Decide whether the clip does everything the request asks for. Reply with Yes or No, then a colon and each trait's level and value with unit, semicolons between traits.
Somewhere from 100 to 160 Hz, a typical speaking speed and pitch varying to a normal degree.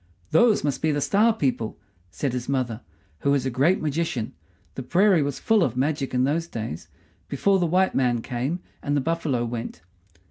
Yes: medium, 140 Hz; average, 185 wpm; average, 5.0 semitones